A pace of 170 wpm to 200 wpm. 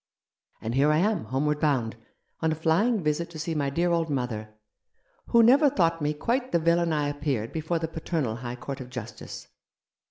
Yes: average, 195 wpm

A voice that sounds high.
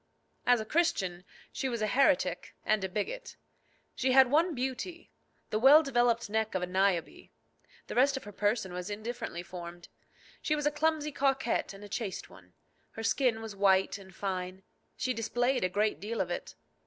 Yes: high, 220 Hz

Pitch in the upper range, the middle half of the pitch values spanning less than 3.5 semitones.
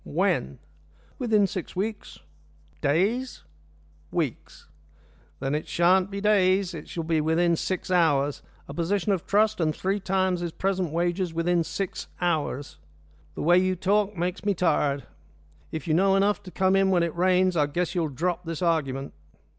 No: medium, 180 Hz; average, 2.9 semitones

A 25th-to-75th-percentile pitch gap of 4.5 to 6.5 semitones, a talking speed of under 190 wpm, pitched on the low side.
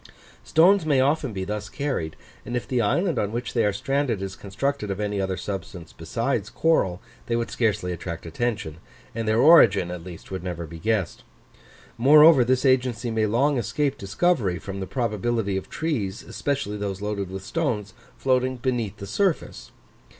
Yes: average, 5.2 semitones; average, 170 wpm; low, 110 Hz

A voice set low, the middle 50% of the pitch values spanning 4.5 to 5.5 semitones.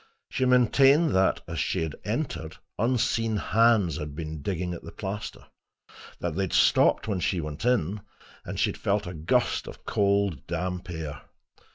Yes: very low, 95 Hz; average, 5.0 semitones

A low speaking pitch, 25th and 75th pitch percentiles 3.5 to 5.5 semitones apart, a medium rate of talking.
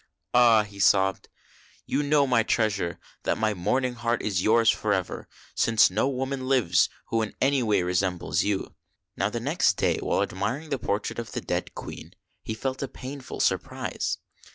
Yes: low, 115 Hz; average, 4.5 semitones; average, 170 wpm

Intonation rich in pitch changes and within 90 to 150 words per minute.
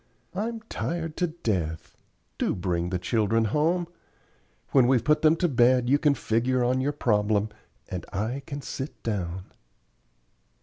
Yes: wide, 6.5 semitones; average, 145 wpm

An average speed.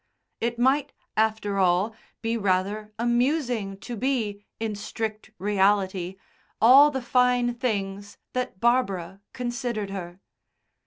No: slow, 110 wpm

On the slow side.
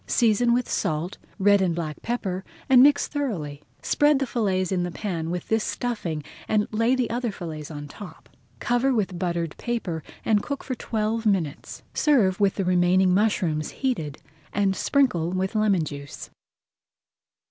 No: average, 160 wpm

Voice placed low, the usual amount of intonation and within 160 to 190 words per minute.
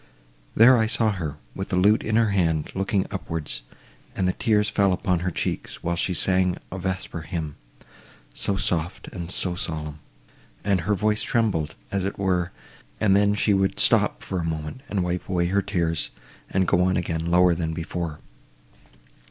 Yes: very low, 90 Hz; average, 3.0 semitones; average, 175 wpm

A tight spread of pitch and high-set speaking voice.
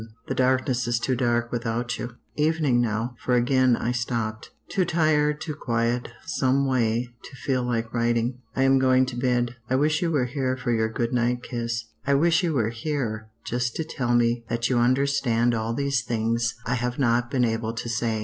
No: narrow, 2.1 semitones; low, 120 Hz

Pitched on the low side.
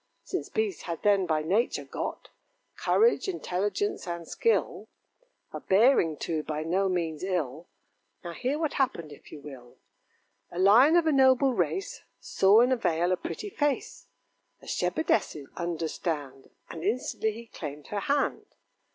No: high, 190 Hz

